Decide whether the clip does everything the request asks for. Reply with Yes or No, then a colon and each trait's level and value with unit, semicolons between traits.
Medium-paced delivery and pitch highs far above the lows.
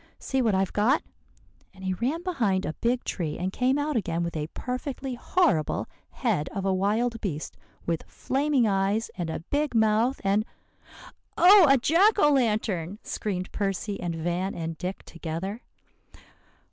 Yes: average, 160 wpm; wide, 6.1 semitones